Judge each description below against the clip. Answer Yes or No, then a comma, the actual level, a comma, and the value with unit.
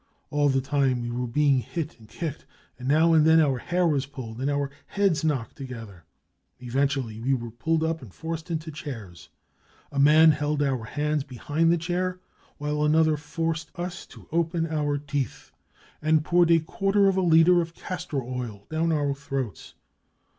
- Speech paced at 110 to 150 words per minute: No, average, 180 wpm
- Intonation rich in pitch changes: No, average, 3.5 semitones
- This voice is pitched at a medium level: Yes, medium, 150 Hz